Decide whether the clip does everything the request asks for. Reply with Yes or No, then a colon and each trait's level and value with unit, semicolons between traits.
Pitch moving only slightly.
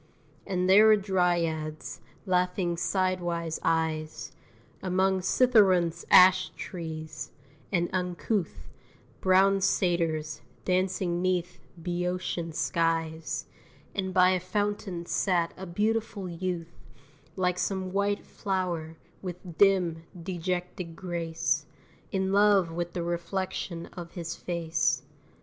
Yes: narrow, 2.1 semitones